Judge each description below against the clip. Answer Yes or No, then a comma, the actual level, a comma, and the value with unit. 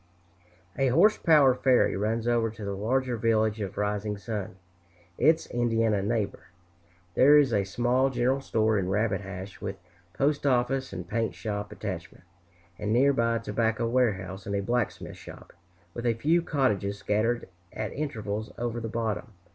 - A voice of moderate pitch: No, low, 115 Hz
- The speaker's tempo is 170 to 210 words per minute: No, average, 155 wpm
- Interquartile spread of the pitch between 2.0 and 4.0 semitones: Yes, average, 3.5 semitones